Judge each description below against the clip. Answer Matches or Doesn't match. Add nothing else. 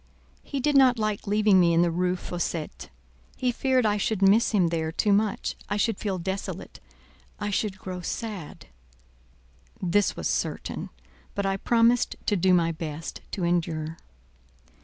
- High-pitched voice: Matches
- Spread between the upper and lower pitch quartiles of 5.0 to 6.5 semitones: Doesn't match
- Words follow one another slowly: Doesn't match